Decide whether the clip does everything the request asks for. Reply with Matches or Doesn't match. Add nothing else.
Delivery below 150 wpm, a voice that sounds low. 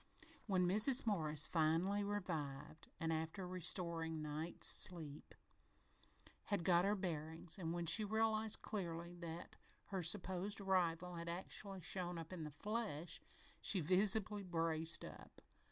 Doesn't match